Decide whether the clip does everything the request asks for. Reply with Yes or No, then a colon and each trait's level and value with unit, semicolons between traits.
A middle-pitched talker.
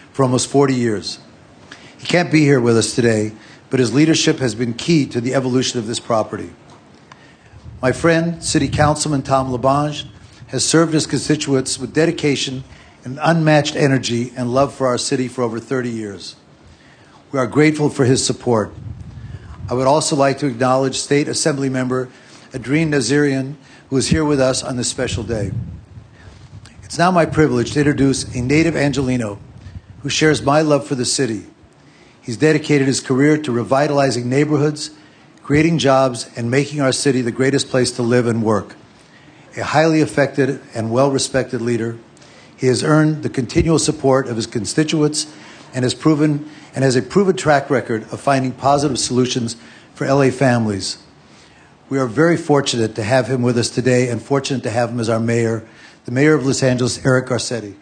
No: low, 130 Hz